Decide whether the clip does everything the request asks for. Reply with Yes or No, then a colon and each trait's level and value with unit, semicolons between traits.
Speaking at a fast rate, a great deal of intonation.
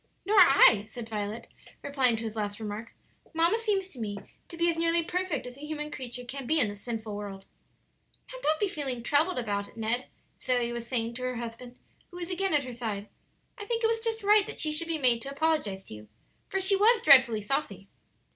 Yes: fast, 220 wpm; wide, 6.8 semitones